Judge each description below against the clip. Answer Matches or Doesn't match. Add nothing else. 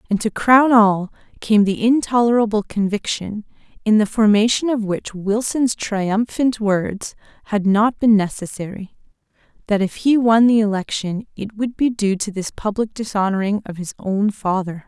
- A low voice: Doesn't match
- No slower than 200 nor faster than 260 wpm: Doesn't match